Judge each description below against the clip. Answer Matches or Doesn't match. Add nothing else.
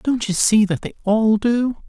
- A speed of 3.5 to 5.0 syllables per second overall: Matches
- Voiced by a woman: Doesn't match